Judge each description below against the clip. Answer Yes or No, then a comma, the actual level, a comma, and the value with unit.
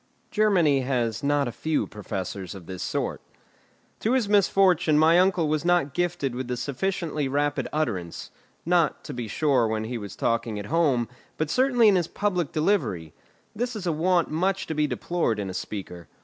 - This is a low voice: No, medium, 150 Hz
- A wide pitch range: Yes, wide, 7.1 semitones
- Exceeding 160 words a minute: Yes, average, 180 wpm